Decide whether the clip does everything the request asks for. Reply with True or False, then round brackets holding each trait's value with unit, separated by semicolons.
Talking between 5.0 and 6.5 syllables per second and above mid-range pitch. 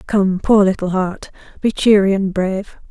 False (4.7 syllables/s; 195 Hz)